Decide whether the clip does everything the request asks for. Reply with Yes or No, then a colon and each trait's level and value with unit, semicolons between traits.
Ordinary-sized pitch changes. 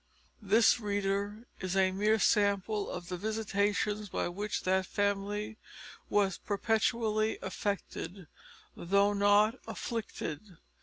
No: narrow, 1.5 semitones